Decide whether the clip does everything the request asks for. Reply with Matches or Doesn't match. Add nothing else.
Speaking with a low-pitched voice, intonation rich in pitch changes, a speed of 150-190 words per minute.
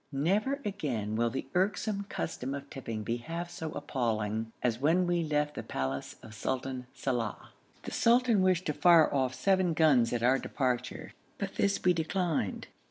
Doesn't match